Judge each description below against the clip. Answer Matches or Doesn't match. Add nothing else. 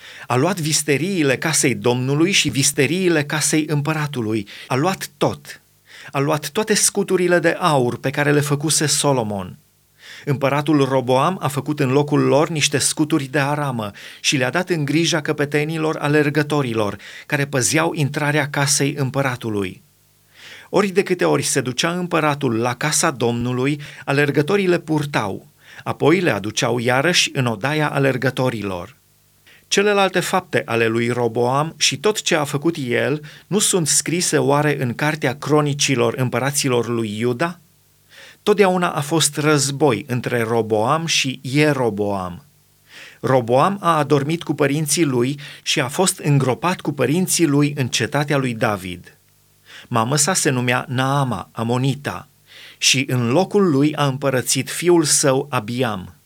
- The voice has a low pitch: Doesn't match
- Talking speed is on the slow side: Doesn't match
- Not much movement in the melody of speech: Doesn't match